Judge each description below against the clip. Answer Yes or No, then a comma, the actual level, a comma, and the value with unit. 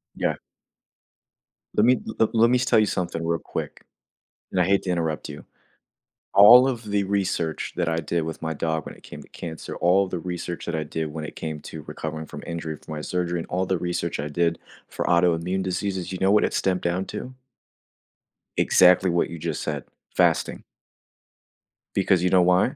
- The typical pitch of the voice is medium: No, very low, 90 Hz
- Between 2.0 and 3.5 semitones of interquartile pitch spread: Yes, average, 2.7 semitones